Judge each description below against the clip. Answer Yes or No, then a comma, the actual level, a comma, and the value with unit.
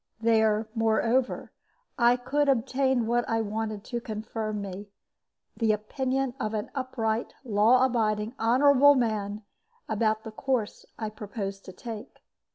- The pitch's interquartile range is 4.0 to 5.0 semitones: No, average, 2.7 semitones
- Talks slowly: Yes, slow, 130 wpm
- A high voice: Yes, high, 225 Hz